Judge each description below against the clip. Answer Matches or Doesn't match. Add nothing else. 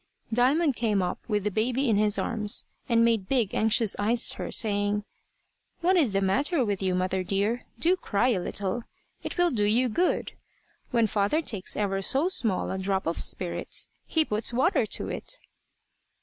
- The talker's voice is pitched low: Doesn't match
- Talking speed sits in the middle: Matches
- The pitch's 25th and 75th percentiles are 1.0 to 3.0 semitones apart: Doesn't match